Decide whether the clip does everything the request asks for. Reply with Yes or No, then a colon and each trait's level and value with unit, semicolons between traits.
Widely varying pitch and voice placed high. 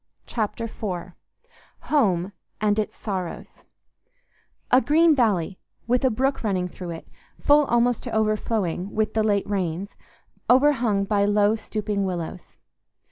No: average, 3.7 semitones; high, 210 Hz